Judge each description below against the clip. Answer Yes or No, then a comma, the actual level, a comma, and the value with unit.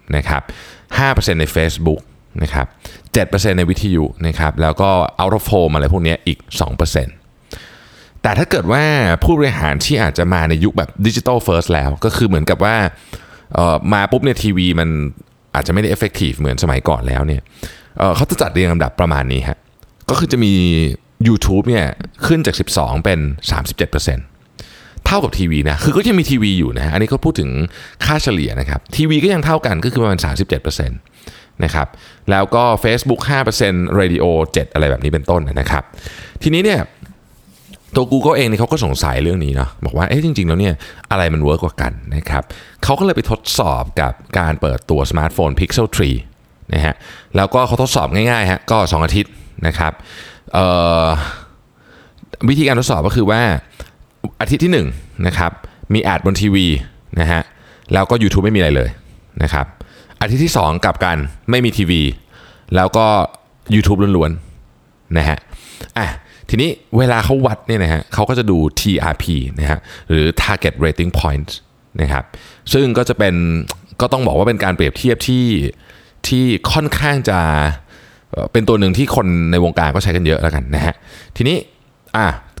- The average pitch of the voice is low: Yes, very low, 90 Hz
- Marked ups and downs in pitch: Yes, wide, 6.3 semitones